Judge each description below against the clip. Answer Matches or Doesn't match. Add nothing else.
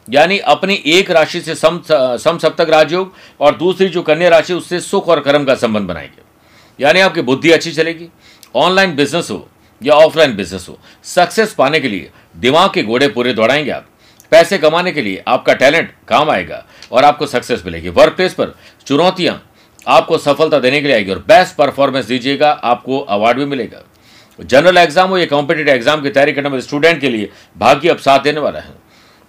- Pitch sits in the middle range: Matches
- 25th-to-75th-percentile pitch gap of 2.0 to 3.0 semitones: Doesn't match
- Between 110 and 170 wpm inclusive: Doesn't match